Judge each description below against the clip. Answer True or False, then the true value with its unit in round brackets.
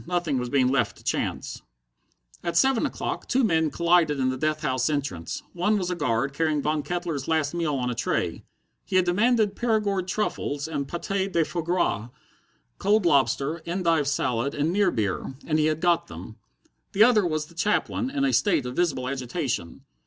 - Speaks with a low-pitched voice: False (160 Hz)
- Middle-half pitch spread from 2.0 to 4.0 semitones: False (4.8 semitones)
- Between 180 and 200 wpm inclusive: True (185 wpm)